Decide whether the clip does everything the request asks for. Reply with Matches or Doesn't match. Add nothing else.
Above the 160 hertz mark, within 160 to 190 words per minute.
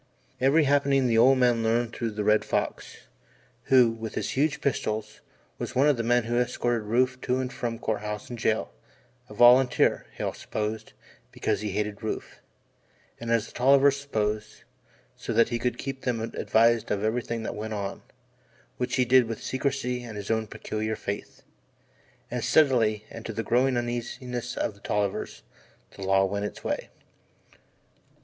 Doesn't match